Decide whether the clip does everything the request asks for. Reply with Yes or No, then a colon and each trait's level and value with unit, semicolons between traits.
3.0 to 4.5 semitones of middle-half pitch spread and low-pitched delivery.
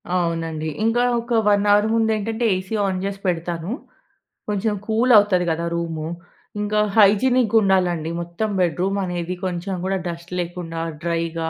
No: average, 3.6 semitones; medium, 185 Hz